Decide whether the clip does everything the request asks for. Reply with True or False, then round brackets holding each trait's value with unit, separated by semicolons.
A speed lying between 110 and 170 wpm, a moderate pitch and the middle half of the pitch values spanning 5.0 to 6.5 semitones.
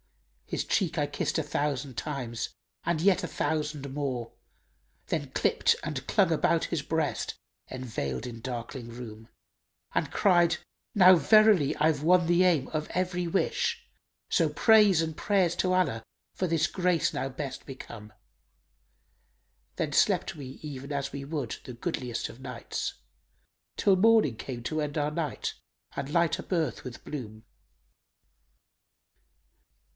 True (145 wpm; 150 Hz; 5.3 semitones)